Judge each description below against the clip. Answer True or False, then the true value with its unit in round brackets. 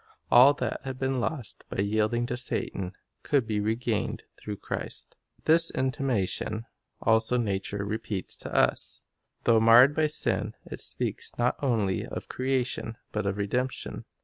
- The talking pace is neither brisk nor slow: True (145 wpm)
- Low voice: True (115 Hz)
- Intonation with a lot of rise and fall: False (3.6 semitones)